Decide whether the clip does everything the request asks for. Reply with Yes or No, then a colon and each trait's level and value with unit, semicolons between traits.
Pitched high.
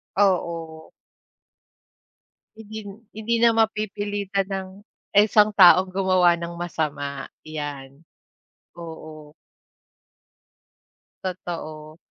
No: medium, 180 Hz